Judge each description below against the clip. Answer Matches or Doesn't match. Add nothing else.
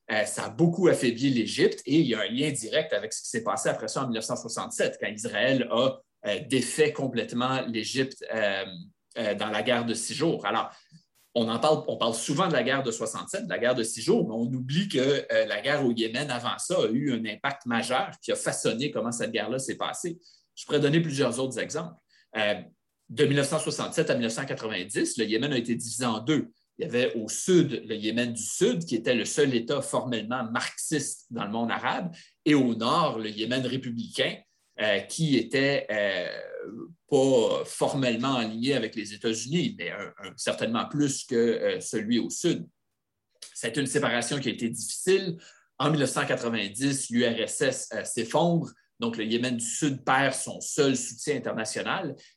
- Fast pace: Doesn't match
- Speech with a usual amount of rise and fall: Matches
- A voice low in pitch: Matches